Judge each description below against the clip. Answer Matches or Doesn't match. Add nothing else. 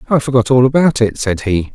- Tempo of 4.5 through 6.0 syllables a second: Matches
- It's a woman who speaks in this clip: Doesn't match